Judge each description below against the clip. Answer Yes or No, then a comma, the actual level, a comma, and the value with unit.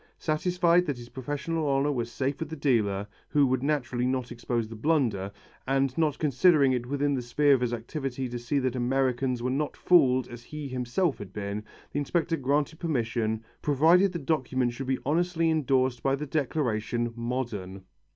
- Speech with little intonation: No, average, 3.7 semitones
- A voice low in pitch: Yes, low, 130 Hz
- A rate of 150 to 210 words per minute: Yes, average, 180 wpm